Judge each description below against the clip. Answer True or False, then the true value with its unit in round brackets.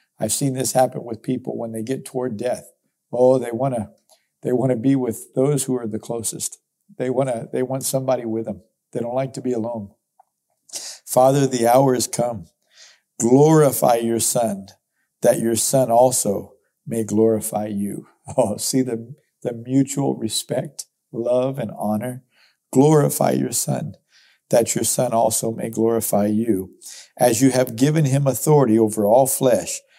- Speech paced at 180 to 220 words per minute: False (160 wpm)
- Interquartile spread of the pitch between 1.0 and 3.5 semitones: True (2.9 semitones)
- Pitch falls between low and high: False (125 Hz)